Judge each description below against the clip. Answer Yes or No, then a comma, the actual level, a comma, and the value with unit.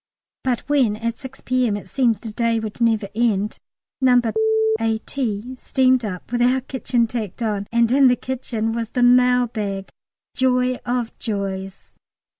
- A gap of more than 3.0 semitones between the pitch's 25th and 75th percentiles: No, average, 2.7 semitones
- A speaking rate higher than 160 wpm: No, average, 155 wpm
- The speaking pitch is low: No, high, 235 Hz